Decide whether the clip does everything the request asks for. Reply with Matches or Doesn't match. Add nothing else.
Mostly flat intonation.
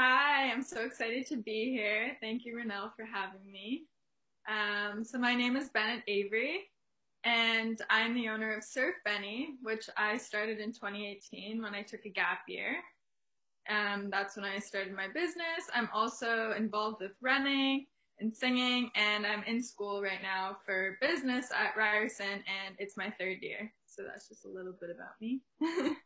Doesn't match